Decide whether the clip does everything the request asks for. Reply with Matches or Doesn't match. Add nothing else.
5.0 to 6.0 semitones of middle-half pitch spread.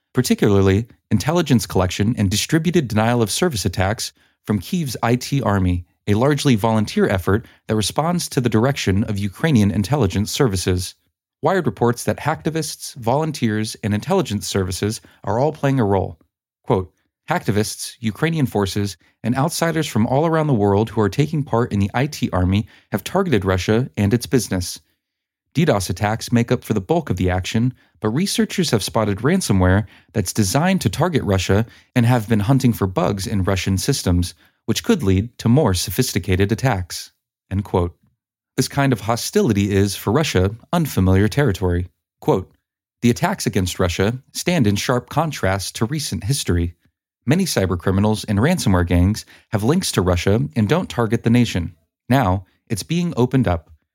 Matches